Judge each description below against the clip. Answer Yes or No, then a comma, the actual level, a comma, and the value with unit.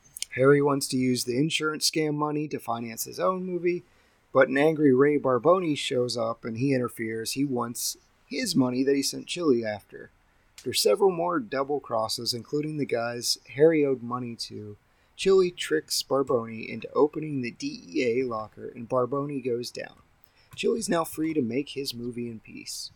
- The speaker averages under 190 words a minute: Yes, average, 170 wpm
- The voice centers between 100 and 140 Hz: Yes, low, 135 Hz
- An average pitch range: Yes, average, 4.0 semitones